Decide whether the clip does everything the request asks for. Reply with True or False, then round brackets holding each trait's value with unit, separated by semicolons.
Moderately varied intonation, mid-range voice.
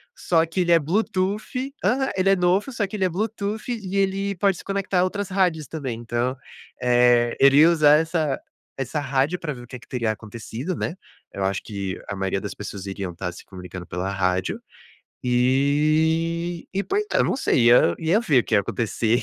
False (8.2 semitones; 150 Hz)